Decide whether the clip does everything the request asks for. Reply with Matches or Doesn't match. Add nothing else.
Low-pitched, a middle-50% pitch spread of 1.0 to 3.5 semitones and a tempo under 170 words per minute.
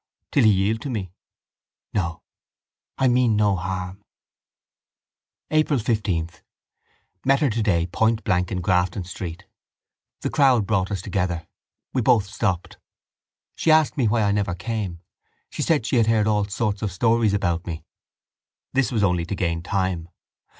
Doesn't match